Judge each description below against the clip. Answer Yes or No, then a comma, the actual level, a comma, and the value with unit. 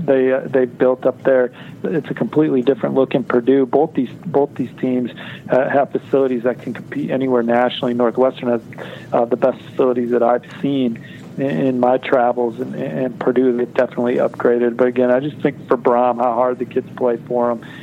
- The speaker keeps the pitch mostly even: Yes, narrow, 1.5 semitones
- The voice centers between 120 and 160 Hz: Yes, low, 125 Hz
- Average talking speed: Yes, average, 195 wpm